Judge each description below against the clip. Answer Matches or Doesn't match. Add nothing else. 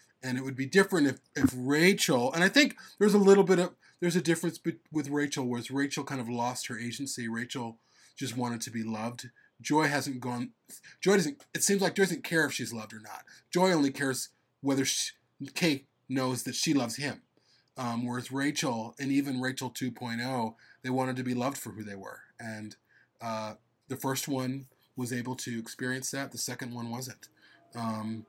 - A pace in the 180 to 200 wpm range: Matches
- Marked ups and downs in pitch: Doesn't match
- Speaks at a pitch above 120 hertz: Matches